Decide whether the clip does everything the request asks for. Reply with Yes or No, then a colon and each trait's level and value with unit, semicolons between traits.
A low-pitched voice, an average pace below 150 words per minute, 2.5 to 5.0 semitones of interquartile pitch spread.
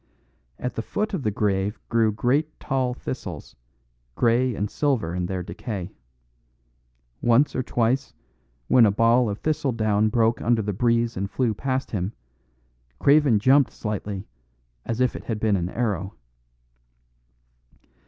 Yes: low, 115 Hz; average, 140 wpm; average, 3.7 semitones